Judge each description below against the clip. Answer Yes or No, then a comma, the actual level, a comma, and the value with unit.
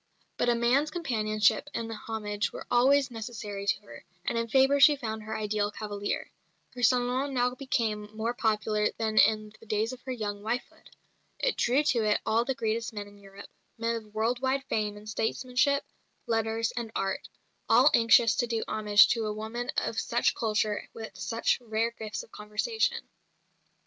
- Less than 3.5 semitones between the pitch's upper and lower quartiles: Yes, narrow, 2.5 semitones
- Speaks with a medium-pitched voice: No, high, 225 Hz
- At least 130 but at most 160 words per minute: No, average, 180 wpm